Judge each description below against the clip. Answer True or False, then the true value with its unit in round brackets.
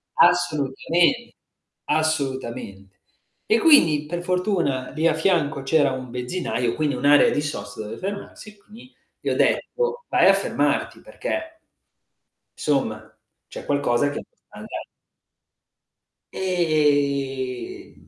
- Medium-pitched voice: True (150 Hz)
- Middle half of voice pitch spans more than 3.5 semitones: True (5.5 semitones)